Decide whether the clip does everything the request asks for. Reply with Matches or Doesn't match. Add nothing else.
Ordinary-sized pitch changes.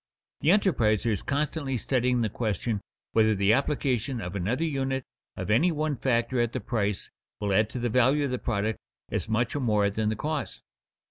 Matches